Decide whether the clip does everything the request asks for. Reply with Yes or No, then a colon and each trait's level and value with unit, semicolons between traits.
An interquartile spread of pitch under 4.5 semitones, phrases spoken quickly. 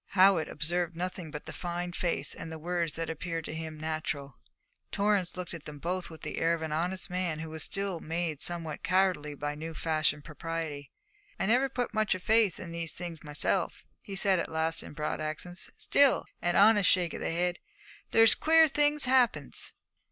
No: average, 3.1 semitones; average, 195 wpm